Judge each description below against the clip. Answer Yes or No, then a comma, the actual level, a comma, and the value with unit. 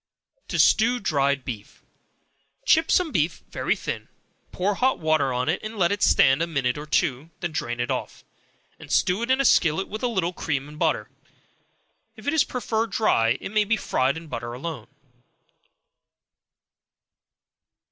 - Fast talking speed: No, average, 165 wpm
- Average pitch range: No, wide, 8.0 semitones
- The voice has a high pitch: No, medium, 165 Hz